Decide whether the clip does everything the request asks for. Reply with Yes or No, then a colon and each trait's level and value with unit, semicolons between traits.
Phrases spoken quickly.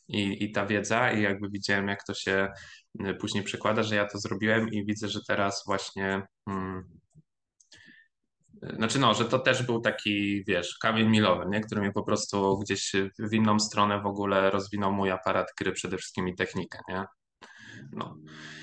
Yes: fast, 170 wpm